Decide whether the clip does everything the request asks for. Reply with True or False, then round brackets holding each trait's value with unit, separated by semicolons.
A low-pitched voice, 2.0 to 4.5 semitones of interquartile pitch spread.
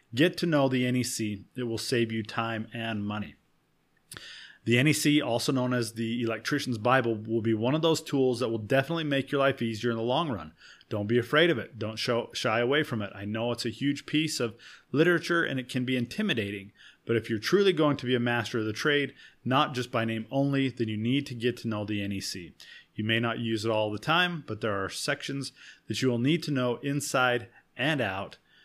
True (120 Hz; 3.7 semitones)